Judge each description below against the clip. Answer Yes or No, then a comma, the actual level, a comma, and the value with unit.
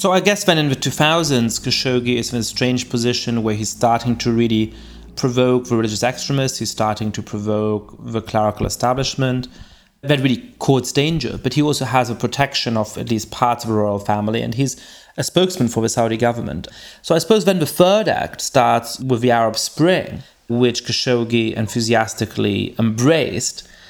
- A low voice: Yes, low, 120 Hz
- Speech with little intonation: No, average, 3.2 semitones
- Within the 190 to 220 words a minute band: No, average, 180 wpm